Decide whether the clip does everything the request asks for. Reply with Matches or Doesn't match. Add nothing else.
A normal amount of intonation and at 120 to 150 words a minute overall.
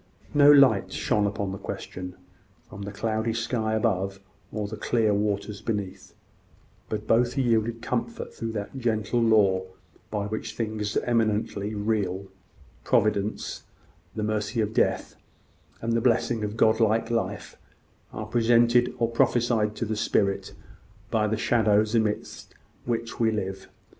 Doesn't match